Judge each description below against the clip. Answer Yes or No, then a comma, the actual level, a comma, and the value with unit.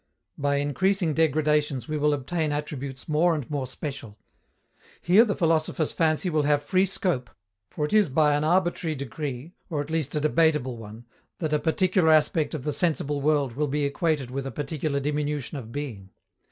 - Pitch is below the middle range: No, medium, 150 Hz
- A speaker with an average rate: Yes, average, 180 wpm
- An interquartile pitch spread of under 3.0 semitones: Yes, narrow, 2.4 semitones